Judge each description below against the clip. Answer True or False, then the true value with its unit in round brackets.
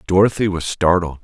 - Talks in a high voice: False (90 Hz)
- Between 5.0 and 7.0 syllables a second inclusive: True (5.6 syllables/s)